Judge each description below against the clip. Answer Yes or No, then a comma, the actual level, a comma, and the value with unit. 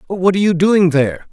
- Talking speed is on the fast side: Yes, fast, 225 wpm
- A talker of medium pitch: Yes, medium, 180 Hz